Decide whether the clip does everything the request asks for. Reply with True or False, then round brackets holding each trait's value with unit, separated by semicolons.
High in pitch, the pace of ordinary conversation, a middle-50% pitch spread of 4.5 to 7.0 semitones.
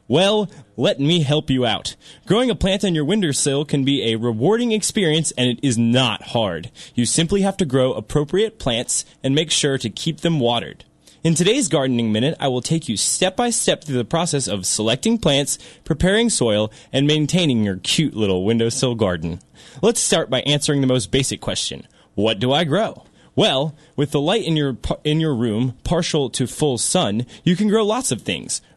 False (145 Hz; 195 wpm; 5.2 semitones)